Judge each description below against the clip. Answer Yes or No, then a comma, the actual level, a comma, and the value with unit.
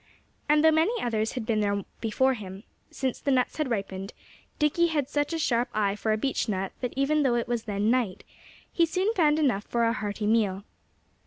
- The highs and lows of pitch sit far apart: Yes, wide, 5.9 semitones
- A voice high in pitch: Yes, high, 240 Hz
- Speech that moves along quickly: Yes, fast, 210 wpm